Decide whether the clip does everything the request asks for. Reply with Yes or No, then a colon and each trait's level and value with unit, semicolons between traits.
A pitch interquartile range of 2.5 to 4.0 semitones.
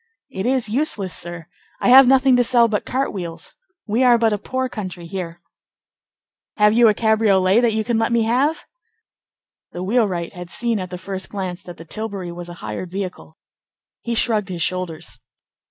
No: average, 4.7 semitones